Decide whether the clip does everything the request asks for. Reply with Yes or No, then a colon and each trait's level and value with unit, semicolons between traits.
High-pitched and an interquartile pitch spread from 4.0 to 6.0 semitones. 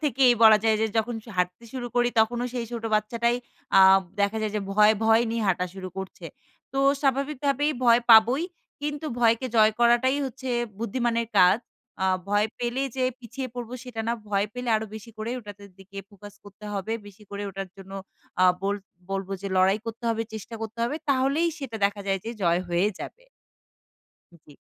No: high, 225 Hz; average, 3.4 semitones